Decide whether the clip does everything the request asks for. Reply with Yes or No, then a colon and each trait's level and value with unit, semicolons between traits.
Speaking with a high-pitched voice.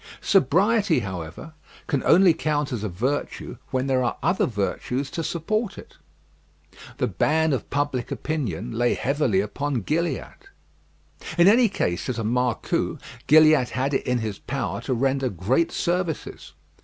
No: low, 135 Hz